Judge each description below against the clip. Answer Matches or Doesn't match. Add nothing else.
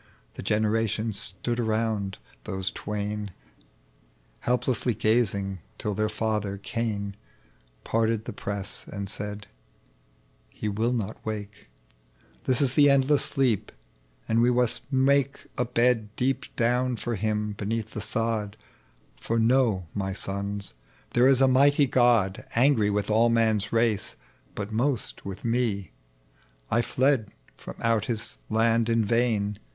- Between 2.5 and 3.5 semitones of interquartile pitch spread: Matches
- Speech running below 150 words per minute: Matches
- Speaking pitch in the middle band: Doesn't match